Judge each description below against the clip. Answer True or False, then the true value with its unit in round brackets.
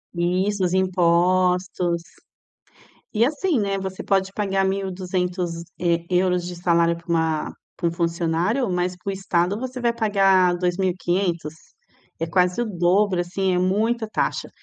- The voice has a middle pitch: True (180 Hz)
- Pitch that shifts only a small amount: True (2.0 semitones)